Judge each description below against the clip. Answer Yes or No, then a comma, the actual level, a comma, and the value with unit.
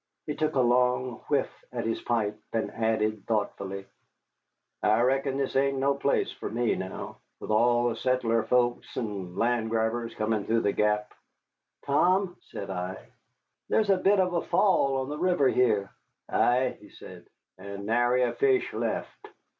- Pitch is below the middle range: Yes, low, 120 Hz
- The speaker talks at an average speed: Yes, average, 160 wpm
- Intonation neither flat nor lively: Yes, average, 4.0 semitones